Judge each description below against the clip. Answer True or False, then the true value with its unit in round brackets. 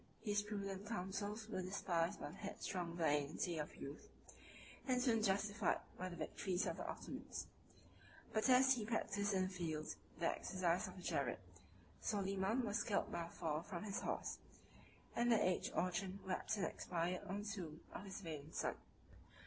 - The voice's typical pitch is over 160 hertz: True (190 Hz)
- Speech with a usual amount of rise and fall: True (3.2 semitones)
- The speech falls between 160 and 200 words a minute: True (170 wpm)